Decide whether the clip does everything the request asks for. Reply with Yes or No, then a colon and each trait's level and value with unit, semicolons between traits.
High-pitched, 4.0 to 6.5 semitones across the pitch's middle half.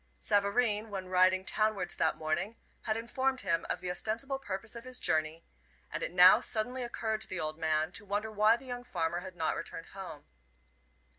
Yes: high, 205 Hz; average, 4.6 semitones